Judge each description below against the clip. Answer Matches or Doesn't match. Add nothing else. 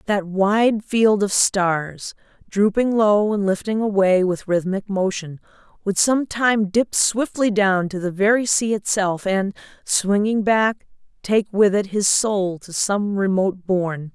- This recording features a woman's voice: Matches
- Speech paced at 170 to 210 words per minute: Doesn't match